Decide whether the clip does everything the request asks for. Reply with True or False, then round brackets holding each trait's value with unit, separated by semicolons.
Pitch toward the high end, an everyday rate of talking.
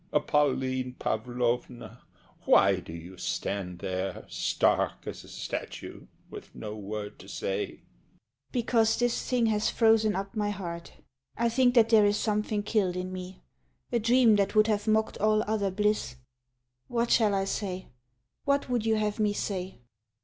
True (205 Hz; 155 wpm)